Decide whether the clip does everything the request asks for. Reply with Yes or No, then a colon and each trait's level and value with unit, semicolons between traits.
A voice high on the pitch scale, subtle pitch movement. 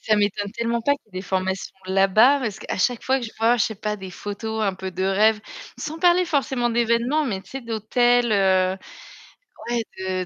No: high, 220 Hz; average, 3.8 semitones